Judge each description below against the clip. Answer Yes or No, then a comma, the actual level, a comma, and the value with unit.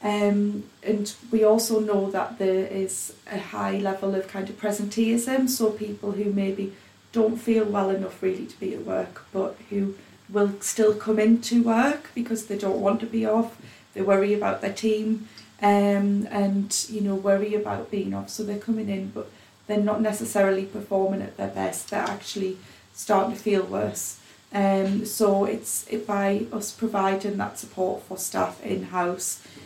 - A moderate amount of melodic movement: No, narrow, 1.7 semitones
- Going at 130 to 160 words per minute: No, average, 170 wpm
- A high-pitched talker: Yes, high, 205 Hz